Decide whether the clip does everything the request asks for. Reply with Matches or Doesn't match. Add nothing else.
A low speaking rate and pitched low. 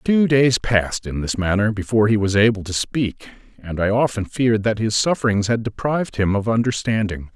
Doesn't match